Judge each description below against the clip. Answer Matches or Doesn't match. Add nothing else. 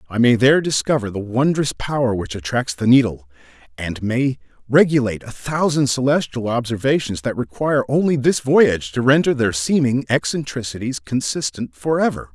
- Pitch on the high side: Doesn't match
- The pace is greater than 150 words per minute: Doesn't match